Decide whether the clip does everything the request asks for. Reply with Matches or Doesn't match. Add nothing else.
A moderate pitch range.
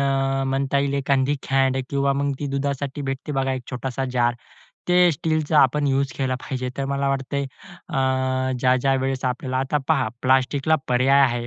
Doesn't match